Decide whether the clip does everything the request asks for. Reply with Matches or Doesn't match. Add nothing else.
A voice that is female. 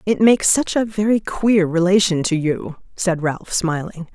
Matches